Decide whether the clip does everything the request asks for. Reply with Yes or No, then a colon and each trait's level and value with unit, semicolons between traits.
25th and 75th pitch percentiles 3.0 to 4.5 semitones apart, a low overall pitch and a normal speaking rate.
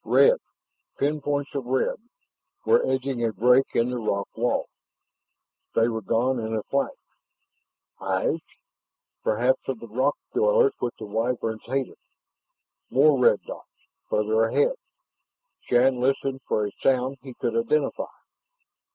No: average, 3.3 semitones; low, 125 Hz; slow, 130 wpm